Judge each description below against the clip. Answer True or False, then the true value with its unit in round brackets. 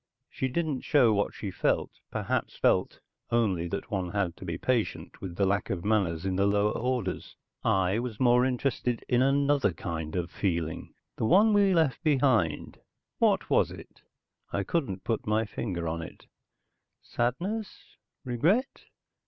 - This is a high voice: False (110 Hz)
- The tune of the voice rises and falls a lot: True (5.8 semitones)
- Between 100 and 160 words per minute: True (155 wpm)